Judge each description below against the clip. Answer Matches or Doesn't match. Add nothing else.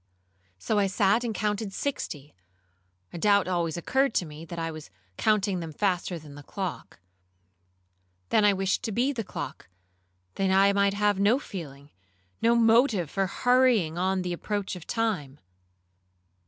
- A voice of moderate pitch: Doesn't match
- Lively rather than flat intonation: Doesn't match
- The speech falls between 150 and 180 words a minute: Matches